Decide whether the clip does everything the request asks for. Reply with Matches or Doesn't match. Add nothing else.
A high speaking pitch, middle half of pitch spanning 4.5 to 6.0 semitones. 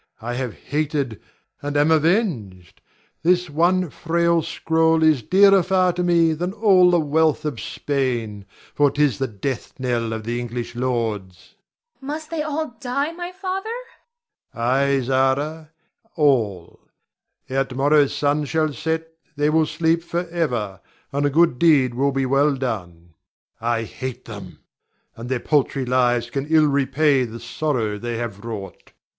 Doesn't match